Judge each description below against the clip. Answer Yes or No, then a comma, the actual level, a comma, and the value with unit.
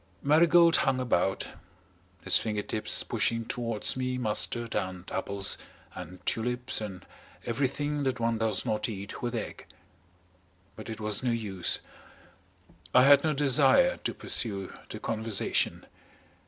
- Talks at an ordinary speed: No, slow, 130 wpm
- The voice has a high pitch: No, low, 115 Hz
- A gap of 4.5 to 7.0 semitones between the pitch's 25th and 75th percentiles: No, average, 3.6 semitones